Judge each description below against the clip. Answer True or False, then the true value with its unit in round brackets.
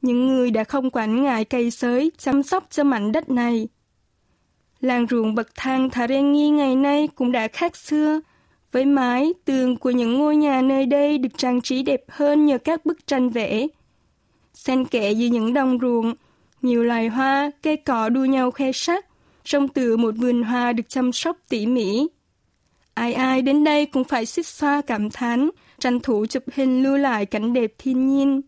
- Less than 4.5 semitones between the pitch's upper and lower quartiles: True (2.8 semitones)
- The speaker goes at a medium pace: True (190 wpm)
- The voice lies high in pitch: True (260 Hz)